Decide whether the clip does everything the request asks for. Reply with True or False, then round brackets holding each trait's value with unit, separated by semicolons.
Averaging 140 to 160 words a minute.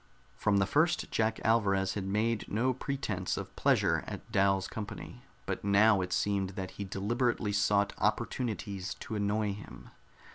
True (150 wpm)